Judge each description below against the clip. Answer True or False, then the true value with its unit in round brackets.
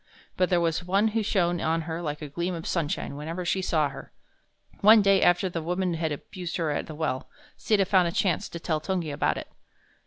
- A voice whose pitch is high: False (170 Hz)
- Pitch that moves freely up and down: False (2.8 semitones)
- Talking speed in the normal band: False (220 wpm)